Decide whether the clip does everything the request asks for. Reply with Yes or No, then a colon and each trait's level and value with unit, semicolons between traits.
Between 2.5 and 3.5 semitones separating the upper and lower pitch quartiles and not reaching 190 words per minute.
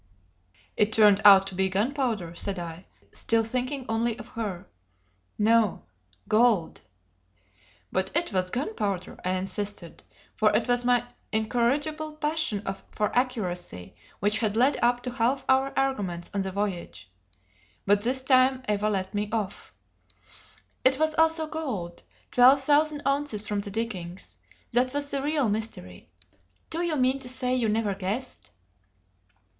No: average, 4.8 semitones; average, 140 wpm